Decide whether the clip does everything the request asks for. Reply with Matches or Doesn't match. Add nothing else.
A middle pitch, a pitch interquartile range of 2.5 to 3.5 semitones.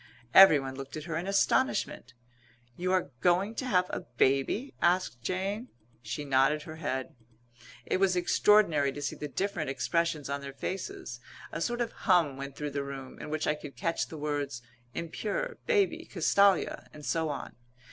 Doesn't match